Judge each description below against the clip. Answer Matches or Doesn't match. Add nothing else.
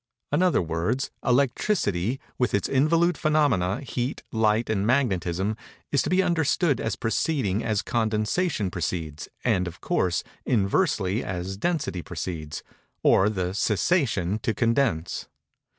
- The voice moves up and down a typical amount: Doesn't match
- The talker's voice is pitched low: Matches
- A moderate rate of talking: Doesn't match